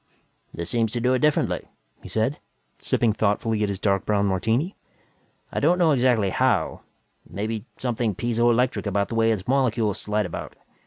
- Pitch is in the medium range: No, low, 115 Hz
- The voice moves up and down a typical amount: Yes, average, 3.3 semitones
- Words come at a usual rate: Yes, average, 170 wpm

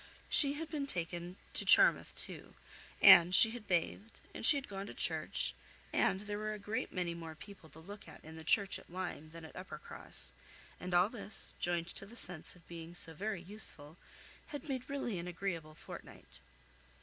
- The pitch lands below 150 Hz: No, medium, 185 Hz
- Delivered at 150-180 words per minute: No, average, 190 wpm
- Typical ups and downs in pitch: Yes, average, 4.1 semitones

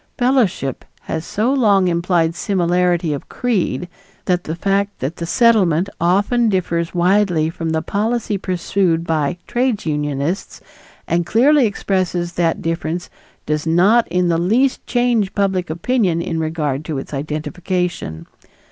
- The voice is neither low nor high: Yes, medium, 180 Hz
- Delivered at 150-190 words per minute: No, slow, 135 wpm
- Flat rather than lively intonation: No, average, 3.7 semitones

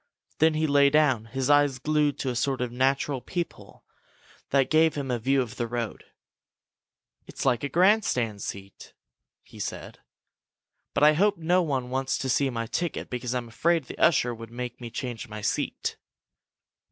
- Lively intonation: No, average, 3.9 semitones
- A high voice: No, low, 135 Hz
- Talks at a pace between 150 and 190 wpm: Yes, average, 175 wpm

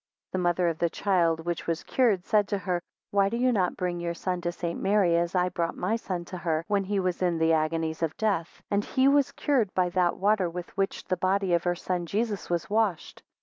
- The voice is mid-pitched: Yes, medium, 180 Hz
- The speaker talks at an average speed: No, fast, 240 wpm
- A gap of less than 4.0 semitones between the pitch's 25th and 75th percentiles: Yes, average, 2.8 semitones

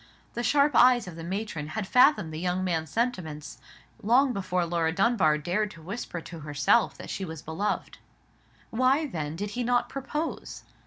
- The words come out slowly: No, average, 170 wpm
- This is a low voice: No, high, 195 Hz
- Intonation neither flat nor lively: No, wide, 7.0 semitones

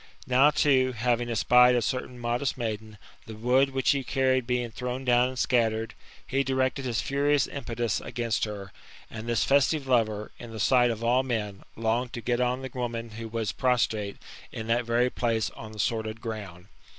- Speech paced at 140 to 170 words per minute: No, average, 185 wpm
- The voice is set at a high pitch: No, low, 120 Hz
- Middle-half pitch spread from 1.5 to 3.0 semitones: Yes, narrow, 2.4 semitones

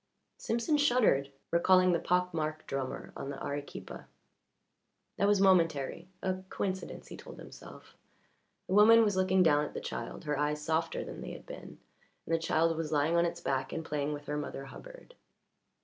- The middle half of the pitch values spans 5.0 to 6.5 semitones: No, average, 4.1 semitones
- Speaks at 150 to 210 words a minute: Yes, average, 180 wpm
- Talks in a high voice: No, medium, 165 Hz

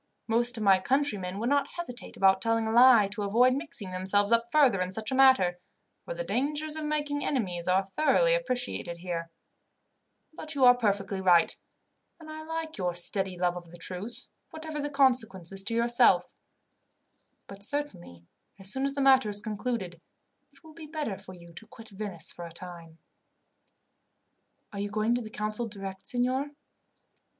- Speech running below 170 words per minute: No, average, 175 wpm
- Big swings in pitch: Yes, wide, 6.2 semitones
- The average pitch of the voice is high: Yes, high, 220 Hz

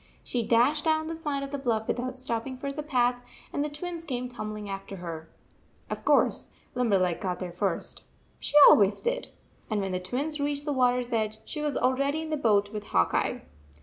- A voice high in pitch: Yes, very high, 250 Hz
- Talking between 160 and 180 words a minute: No, fast, 205 wpm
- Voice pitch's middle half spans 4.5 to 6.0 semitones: Yes, wide, 5.6 semitones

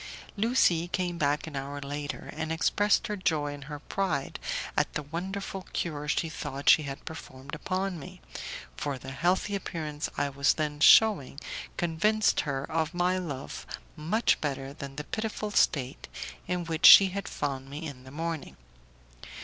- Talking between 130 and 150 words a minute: No, average, 160 wpm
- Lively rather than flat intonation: No, average, 4.2 semitones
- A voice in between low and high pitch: Yes, medium, 155 Hz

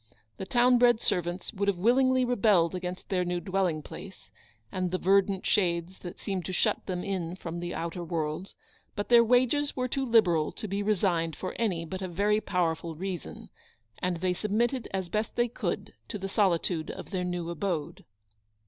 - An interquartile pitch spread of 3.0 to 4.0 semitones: Yes, average, 3.5 semitones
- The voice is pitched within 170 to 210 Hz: Yes, medium, 185 Hz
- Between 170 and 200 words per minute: Yes, average, 190 wpm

